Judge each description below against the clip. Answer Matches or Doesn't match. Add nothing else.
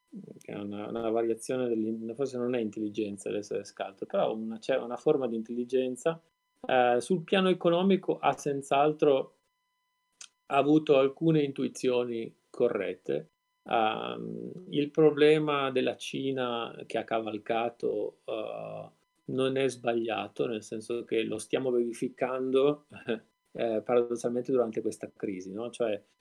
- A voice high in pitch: Doesn't match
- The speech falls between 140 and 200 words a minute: Doesn't match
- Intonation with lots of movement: Matches